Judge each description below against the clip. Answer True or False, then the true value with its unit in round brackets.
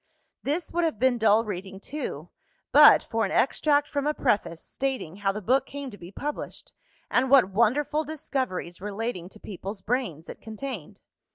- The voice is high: True (230 Hz)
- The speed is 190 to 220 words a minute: False (170 wpm)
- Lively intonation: True (5.9 semitones)